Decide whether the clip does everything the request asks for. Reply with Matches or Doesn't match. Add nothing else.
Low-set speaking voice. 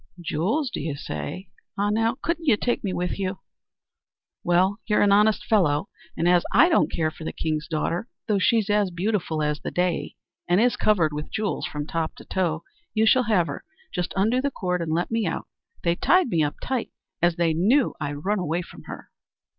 Doesn't match